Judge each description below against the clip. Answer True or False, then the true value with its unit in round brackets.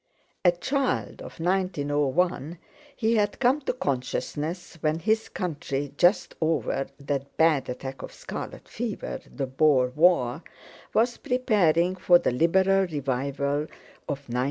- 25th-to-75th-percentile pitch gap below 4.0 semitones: False (5.3 semitones)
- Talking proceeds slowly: True (130 wpm)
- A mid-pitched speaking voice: True (160 Hz)